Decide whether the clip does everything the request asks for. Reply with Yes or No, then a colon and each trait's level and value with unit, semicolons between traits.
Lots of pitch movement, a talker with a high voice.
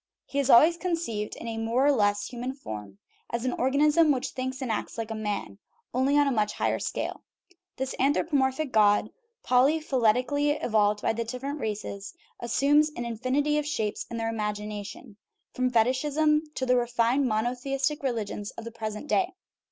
No: average, 4.3 semitones; very high, 250 Hz